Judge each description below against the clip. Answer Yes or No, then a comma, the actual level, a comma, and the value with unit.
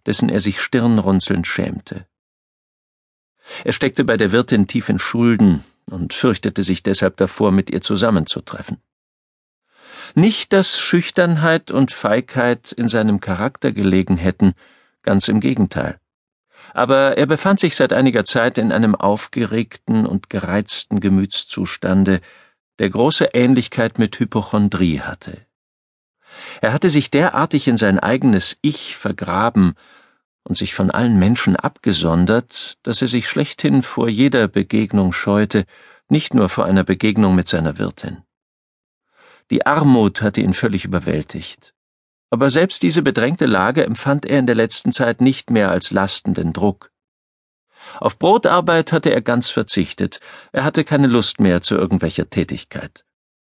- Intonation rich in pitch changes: Yes, wide, 6.1 semitones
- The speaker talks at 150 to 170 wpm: No, average, 135 wpm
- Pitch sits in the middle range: No, low, 110 Hz